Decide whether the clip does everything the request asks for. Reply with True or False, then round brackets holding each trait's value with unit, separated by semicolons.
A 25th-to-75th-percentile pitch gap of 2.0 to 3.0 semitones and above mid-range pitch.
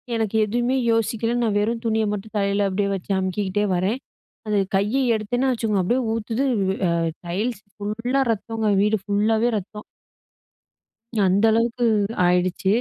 True (2.4 semitones; 215 Hz)